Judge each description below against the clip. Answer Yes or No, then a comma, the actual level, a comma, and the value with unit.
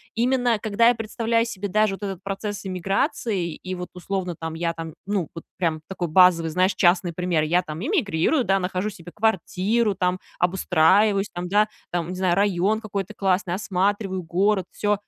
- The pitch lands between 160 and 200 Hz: Yes, high, 190 Hz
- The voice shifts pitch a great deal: No, average, 2.9 semitones